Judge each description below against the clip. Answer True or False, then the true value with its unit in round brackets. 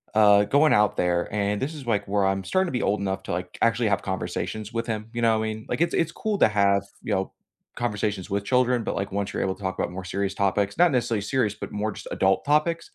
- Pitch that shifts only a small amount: False (3.5 semitones)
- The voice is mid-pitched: False (105 Hz)